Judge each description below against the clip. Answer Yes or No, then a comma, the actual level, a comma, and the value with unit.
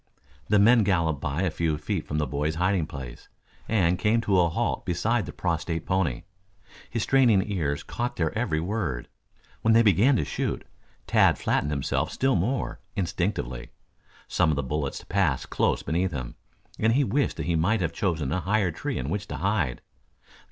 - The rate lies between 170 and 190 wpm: Yes, average, 180 wpm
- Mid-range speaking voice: No, very low, 90 Hz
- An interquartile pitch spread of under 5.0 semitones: No, wide, 5.5 semitones